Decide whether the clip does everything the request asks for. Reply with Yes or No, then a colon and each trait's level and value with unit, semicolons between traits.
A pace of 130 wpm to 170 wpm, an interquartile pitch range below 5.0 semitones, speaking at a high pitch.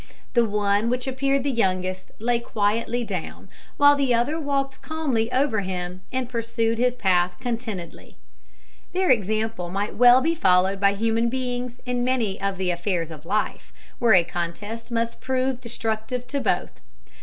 Yes: average, 155 wpm; average, 4.2 semitones; high, 230 Hz